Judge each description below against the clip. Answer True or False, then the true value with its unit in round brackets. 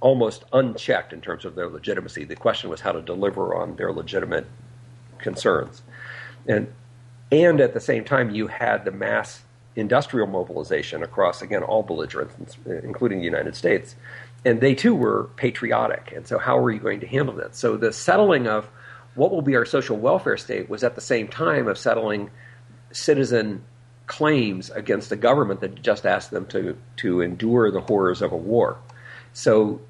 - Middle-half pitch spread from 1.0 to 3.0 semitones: True (2.4 semitones)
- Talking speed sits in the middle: True (175 wpm)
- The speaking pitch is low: True (120 Hz)